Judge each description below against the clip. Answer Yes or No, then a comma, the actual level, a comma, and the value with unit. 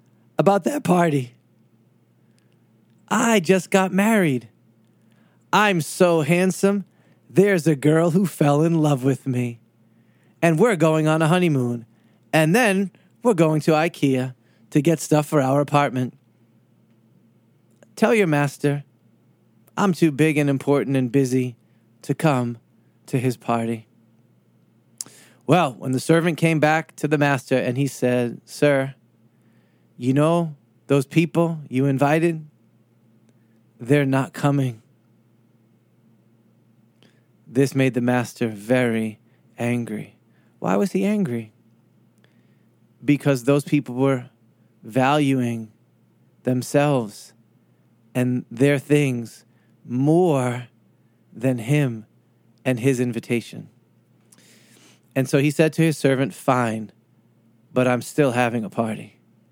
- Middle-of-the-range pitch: No, low, 130 Hz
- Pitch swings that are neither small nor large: Yes, average, 4.7 semitones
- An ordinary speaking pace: No, slow, 115 wpm